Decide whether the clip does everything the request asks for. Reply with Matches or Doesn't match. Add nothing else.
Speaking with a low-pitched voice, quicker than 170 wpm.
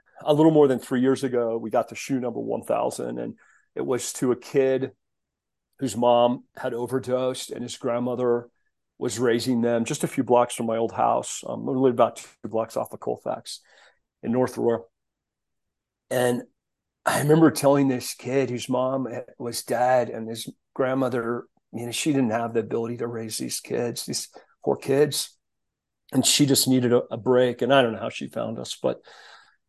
Matches